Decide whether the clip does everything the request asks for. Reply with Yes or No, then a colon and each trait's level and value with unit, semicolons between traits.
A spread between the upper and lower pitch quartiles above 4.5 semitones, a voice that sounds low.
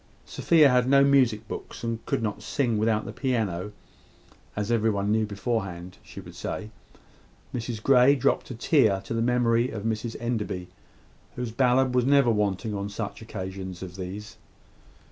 No: average, 3.4 semitones; low, 115 Hz